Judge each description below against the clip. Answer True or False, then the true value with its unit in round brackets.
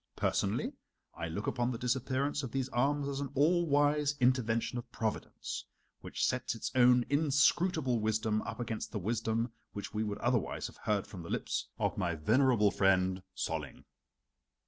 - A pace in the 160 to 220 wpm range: True (165 wpm)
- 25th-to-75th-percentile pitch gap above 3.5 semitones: True (4.3 semitones)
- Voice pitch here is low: True (120 Hz)